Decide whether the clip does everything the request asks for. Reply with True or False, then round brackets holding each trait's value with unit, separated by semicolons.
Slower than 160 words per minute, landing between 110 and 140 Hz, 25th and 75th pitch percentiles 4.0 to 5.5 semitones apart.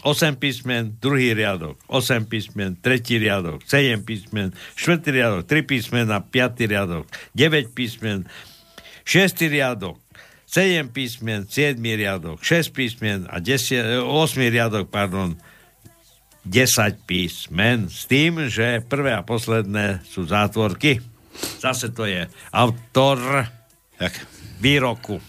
True (115 wpm; 115 Hz; 4.4 semitones)